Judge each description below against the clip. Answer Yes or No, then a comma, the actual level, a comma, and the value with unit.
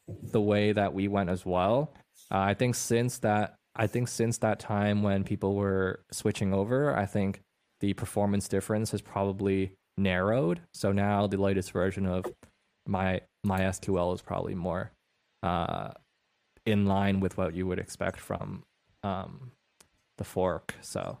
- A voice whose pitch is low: Yes, low, 100 Hz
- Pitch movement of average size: No, narrow, 2.2 semitones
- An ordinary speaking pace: Yes, average, 155 wpm